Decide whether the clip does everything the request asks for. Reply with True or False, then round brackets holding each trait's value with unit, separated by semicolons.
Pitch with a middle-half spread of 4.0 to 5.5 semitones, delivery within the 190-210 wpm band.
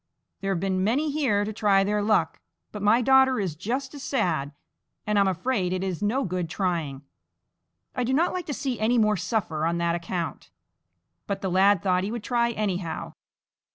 True (4.6 semitones; 195 wpm)